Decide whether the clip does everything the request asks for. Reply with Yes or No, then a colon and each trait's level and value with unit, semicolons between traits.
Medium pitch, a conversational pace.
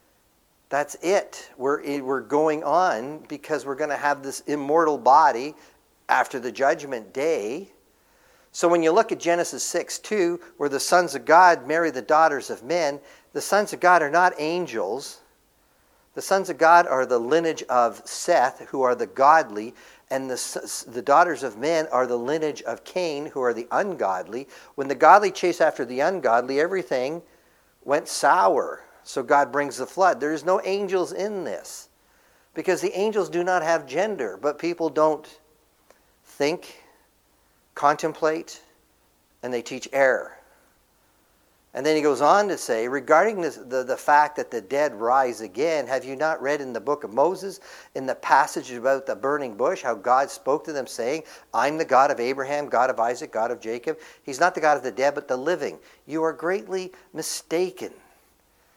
Yes: medium, 155 Hz; average, 175 wpm